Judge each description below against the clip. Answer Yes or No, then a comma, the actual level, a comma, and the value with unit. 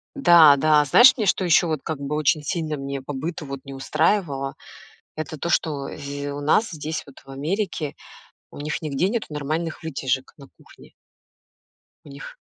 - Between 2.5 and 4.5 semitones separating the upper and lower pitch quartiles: Yes, average, 3.1 semitones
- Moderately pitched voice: Yes, medium, 150 Hz